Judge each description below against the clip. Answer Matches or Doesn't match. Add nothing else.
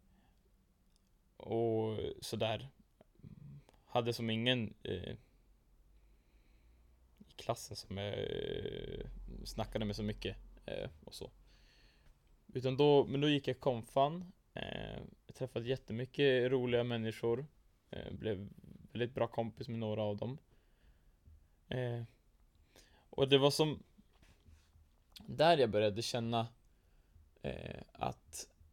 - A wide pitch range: Matches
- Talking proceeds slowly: Matches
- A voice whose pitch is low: Matches